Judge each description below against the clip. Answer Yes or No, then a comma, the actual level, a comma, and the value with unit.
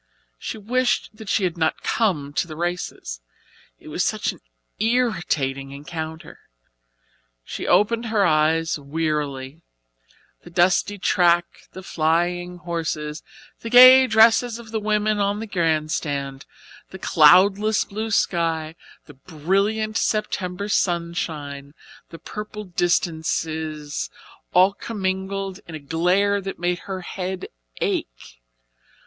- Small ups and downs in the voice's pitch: No, average, 4.6 semitones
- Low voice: No, medium, 175 Hz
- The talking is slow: Yes, slow, 120 wpm